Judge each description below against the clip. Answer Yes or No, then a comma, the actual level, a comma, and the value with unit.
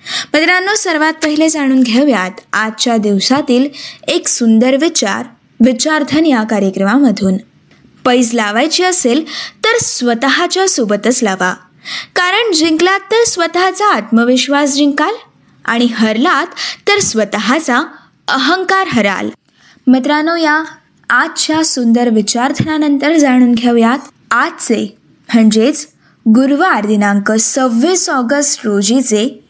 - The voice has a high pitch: Yes, very high, 270 Hz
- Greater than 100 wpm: No, average, 95 wpm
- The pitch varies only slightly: No, wide, 5.4 semitones